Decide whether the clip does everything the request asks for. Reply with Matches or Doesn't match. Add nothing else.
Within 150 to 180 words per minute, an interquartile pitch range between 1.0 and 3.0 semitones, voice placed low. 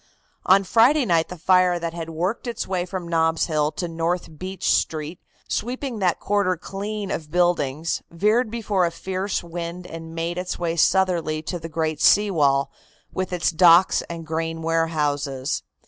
Doesn't match